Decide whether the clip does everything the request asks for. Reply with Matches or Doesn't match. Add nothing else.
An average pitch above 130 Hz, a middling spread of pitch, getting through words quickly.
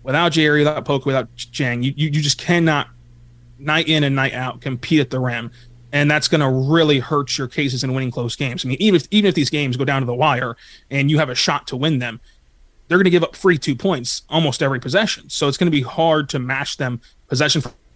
Matches